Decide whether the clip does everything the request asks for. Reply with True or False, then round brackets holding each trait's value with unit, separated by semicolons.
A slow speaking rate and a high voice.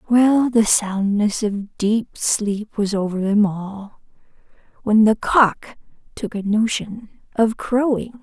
True (130 wpm; 215 Hz)